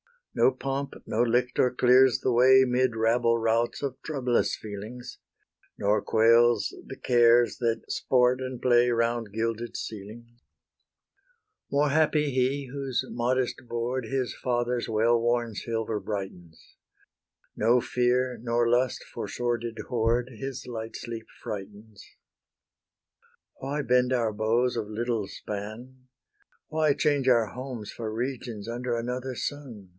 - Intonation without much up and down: Yes, narrow, 2.1 semitones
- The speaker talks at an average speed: No, slow, 125 wpm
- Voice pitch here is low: Yes, low, 120 Hz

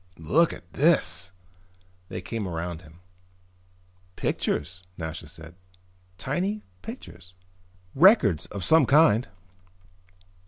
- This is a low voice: Yes, very low, 90 Hz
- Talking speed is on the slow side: Yes, slow, 90 wpm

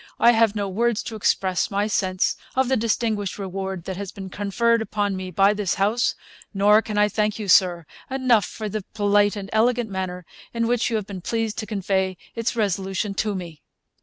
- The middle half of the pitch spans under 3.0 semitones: Yes, narrow, 2.6 semitones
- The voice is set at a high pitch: Yes, high, 205 Hz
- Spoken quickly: No, average, 195 wpm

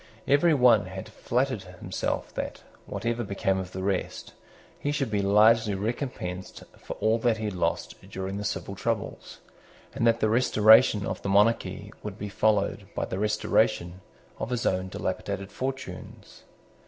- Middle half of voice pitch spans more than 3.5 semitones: No, average, 3.2 semitones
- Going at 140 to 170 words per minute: Yes, average, 155 wpm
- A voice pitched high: No, low, 105 Hz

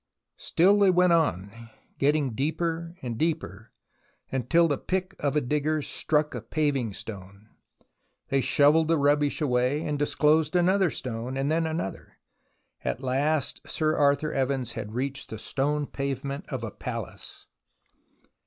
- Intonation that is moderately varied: Yes, average, 3.7 semitones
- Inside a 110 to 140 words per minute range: Yes, slow, 135 wpm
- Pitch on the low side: No, medium, 145 Hz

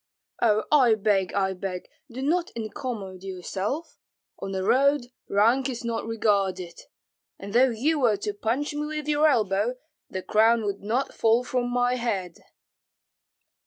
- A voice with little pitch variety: No, average, 4.6 semitones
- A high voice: Yes, high, 225 Hz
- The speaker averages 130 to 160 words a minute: Yes, average, 150 wpm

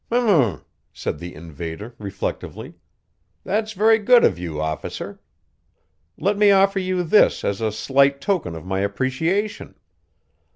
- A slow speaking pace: Yes, slow, 130 wpm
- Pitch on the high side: No, medium, 140 Hz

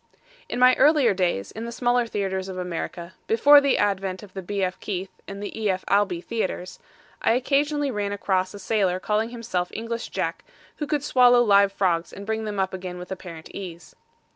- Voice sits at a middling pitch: No, high, 200 Hz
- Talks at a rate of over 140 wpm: Yes, average, 190 wpm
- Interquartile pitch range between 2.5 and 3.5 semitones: No, average, 3.9 semitones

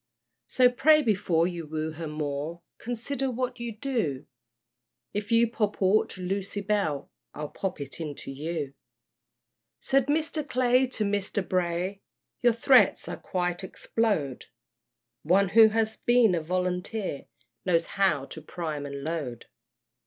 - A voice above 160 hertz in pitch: Yes, high, 190 Hz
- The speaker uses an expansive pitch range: Yes, wide, 6.3 semitones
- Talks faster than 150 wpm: No, average, 140 wpm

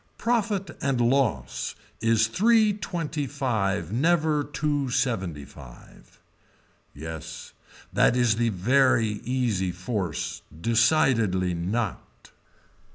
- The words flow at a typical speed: No, slow, 95 wpm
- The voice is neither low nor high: No, low, 120 Hz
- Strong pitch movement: Yes, wide, 7.2 semitones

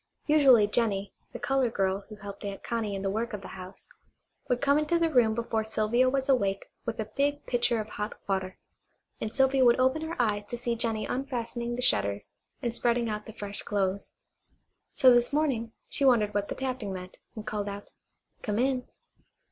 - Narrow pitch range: No, average, 3.8 semitones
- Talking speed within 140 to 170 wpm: No, average, 195 wpm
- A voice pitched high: Yes, high, 230 Hz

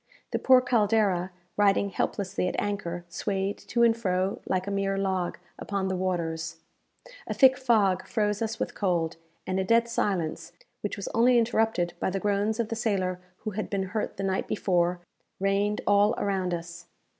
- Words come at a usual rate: Yes, average, 175 wpm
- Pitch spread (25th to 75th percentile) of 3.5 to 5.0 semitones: No, average, 2.9 semitones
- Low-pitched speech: No, high, 195 Hz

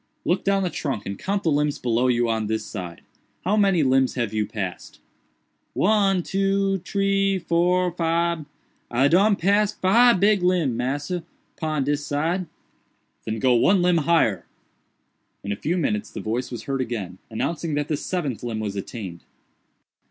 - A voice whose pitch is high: No, medium, 155 Hz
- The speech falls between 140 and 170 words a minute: Yes, average, 160 wpm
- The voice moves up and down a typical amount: No, wide, 7.8 semitones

